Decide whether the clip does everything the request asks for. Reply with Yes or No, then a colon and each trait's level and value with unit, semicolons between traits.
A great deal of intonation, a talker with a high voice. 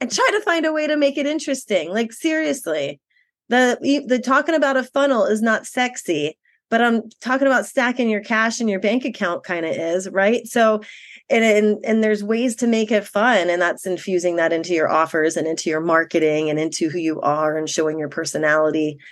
Yes: wide, 7.3 semitones; high, 215 Hz